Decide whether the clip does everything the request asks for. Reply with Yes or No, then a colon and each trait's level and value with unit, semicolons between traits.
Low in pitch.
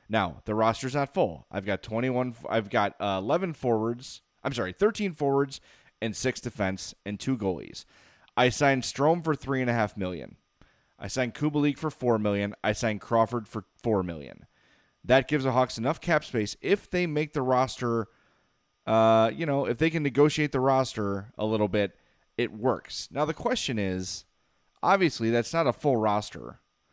Yes: low, 120 Hz